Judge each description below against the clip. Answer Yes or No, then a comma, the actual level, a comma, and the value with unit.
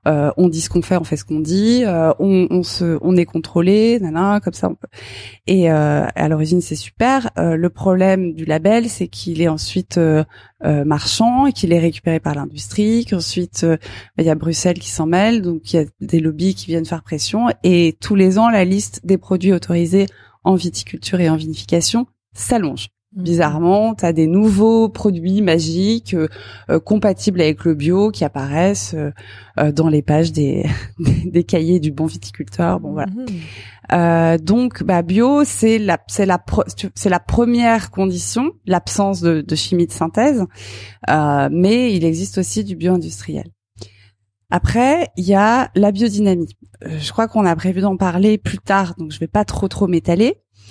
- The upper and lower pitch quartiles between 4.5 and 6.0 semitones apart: No, average, 4.0 semitones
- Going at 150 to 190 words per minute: Yes, average, 185 wpm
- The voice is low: No, medium, 175 Hz